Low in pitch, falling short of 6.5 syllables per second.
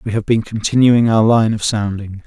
Yes: low, 110 Hz; 5.1 syllables/s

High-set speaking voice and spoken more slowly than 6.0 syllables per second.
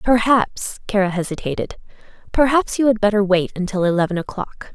Yes: high, 205 Hz; 5.5 syllables/s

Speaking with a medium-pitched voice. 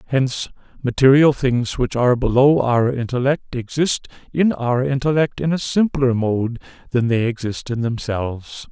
No: low, 130 Hz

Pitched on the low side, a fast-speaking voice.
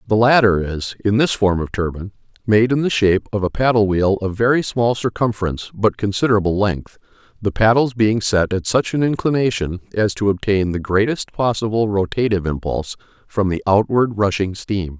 No: low, 105 Hz; average, 175 wpm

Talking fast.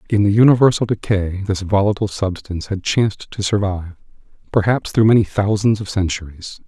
No: average, 155 wpm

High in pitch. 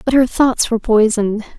Yes: high, 230 Hz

